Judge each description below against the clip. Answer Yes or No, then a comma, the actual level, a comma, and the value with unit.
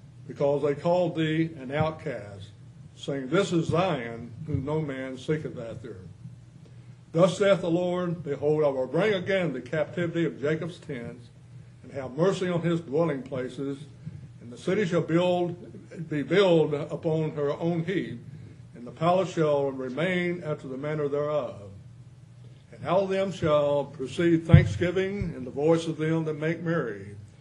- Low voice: No, medium, 150 Hz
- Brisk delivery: No, average, 155 wpm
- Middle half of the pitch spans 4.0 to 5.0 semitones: Yes, average, 4.3 semitones